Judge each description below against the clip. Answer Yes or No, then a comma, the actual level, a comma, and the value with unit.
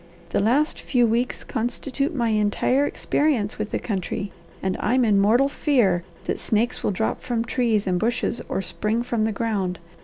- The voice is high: Yes, high, 225 Hz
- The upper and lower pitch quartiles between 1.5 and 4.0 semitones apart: Yes, average, 3.2 semitones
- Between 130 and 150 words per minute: No, average, 175 wpm